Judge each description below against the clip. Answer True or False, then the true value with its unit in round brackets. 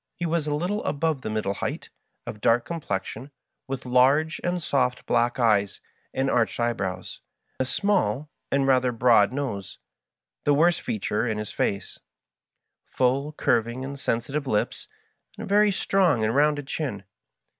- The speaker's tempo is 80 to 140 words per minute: False (155 wpm)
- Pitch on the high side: False (130 Hz)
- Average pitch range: True (4.8 semitones)